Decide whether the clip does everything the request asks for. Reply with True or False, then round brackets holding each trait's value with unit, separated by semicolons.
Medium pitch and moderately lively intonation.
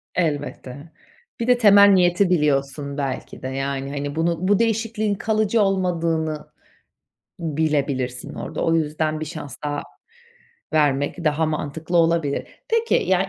True (160 Hz; 4.7 semitones)